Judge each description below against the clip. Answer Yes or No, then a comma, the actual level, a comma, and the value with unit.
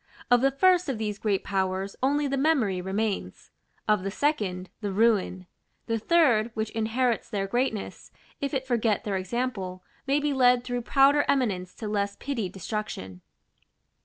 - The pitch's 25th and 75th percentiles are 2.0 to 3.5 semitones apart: No, average, 5.2 semitones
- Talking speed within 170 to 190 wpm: No, average, 160 wpm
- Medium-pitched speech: No, high, 220 Hz